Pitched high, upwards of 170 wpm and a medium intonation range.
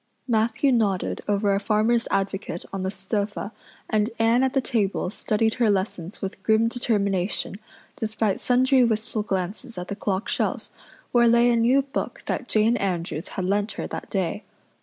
No: high, 215 Hz; average, 165 wpm; average, 3.1 semitones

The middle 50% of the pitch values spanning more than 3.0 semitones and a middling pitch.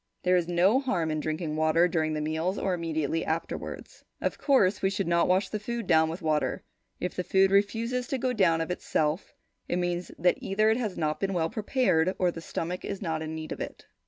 Yes: average, 3.7 semitones; medium, 180 Hz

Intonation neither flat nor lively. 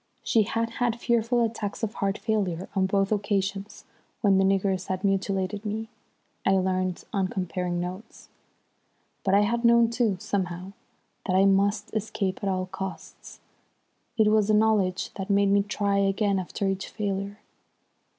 No: narrow, 2.0 semitones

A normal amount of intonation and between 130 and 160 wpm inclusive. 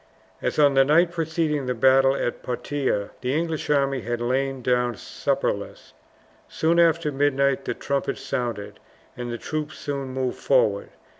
Yes: average, 3.2 semitones; average, 150 wpm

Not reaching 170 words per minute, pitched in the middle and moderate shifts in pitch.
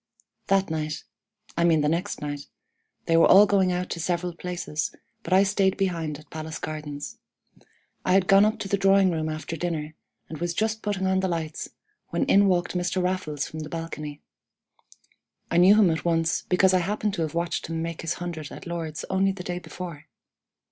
No: average, 195 wpm; medium, 175 Hz; average, 3.0 semitones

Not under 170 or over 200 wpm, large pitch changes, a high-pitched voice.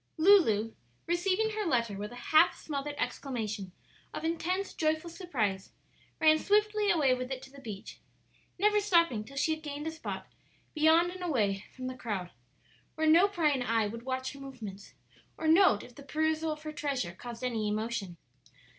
Yes: average, 175 wpm; wide, 6.2 semitones; very high, 285 Hz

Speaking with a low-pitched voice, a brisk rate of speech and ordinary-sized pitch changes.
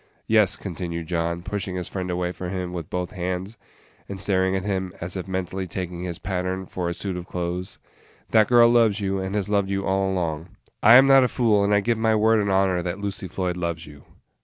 No: very low, 95 Hz; fast, 230 wpm; narrow, 2.2 semitones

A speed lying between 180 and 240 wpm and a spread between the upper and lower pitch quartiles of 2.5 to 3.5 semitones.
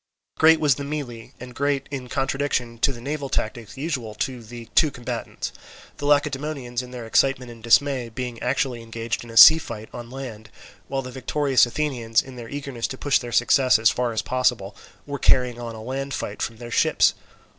Yes: average, 195 wpm; average, 2.9 semitones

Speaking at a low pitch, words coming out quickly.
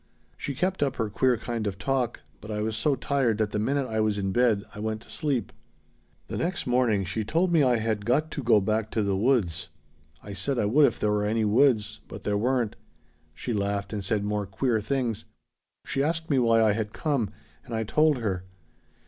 Yes: low, 110 Hz; fast, 215 wpm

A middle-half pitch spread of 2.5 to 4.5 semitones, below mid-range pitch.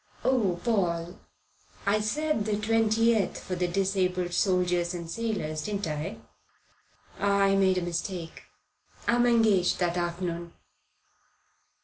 No: average, 3.6 semitones; high, 190 Hz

